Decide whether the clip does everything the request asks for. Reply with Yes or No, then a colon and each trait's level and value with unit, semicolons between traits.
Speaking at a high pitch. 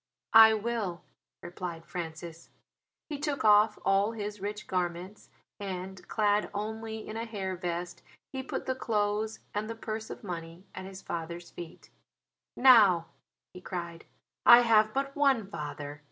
Yes: high, 205 Hz